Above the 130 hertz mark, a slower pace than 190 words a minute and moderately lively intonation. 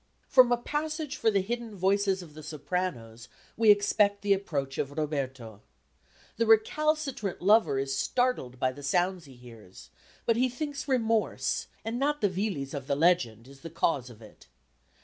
No: medium, 185 Hz; average, 170 wpm; wide, 8.8 semitones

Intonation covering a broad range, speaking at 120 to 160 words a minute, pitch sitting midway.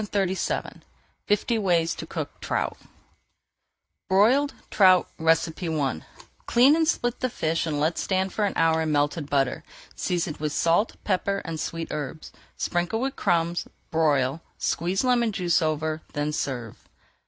No: average, 4.3 semitones; average, 140 wpm; medium, 170 Hz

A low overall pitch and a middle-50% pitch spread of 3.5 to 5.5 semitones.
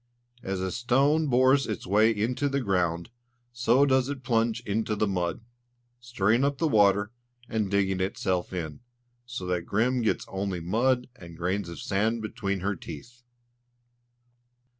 Yes: low, 110 Hz; average, 4.4 semitones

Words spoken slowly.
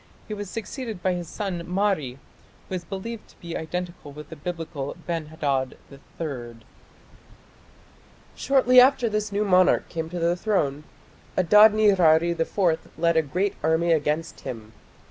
No: average, 145 wpm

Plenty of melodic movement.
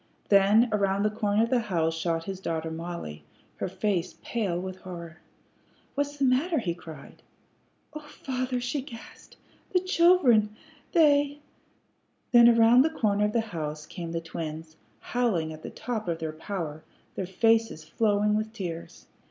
Yes: wide, 6.3 semitones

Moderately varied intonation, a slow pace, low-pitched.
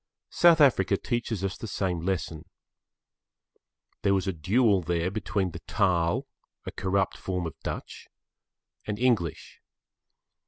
Yes: average, 3.8 semitones; slow, 125 wpm; very low, 95 Hz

